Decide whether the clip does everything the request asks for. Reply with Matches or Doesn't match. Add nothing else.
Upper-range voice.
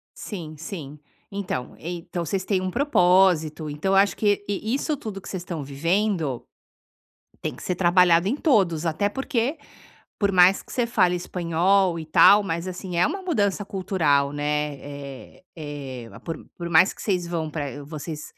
Doesn't match